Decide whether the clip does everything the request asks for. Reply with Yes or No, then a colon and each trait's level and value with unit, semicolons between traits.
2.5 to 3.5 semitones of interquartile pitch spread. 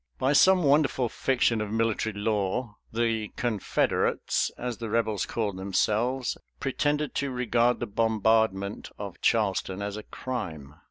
Yes: average, 3.1 semitones